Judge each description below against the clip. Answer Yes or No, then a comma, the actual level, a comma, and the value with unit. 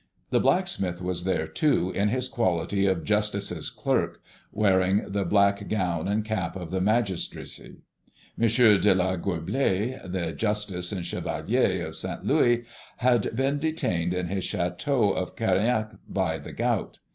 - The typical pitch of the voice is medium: No, low, 100 Hz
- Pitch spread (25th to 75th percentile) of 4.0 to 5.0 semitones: No, average, 3.3 semitones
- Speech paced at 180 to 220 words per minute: No, average, 145 wpm